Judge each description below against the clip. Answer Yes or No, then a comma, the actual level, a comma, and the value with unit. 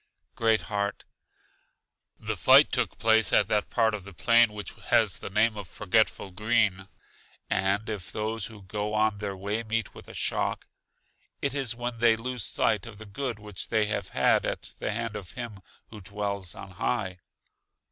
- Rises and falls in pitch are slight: Yes, narrow, 2.2 semitones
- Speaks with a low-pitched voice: Yes, low, 105 Hz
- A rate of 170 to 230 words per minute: Yes, average, 175 wpm